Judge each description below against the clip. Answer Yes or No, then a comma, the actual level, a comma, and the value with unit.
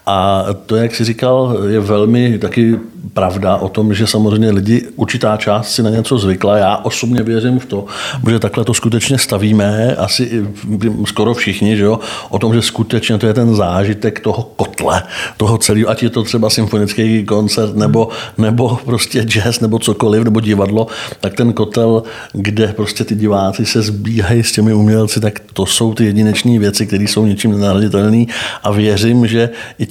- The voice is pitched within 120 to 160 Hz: No, low, 110 Hz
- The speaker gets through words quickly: Yes, fast, 175 wpm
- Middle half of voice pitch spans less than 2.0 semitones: Yes, narrow, 1.6 semitones